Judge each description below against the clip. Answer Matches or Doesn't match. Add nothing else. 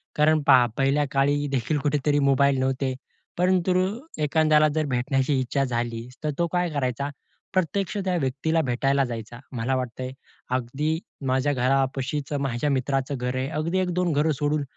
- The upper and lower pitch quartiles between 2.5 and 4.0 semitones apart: Matches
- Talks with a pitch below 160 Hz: Matches